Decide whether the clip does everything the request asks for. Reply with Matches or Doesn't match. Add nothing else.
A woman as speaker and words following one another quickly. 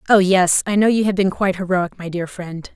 Matches